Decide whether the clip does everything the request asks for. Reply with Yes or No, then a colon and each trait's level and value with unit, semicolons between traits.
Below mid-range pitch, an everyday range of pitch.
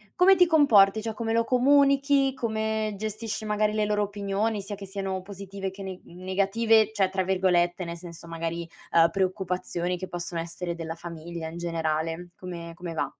No: high, 195 Hz; average, 4.0 semitones